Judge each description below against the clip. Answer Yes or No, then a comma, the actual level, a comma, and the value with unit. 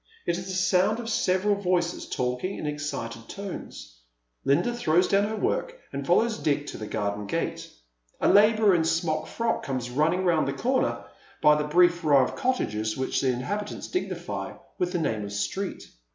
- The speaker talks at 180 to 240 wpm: Yes, average, 185 wpm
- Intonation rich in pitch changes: Yes, wide, 6.8 semitones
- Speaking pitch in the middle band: Yes, medium, 170 Hz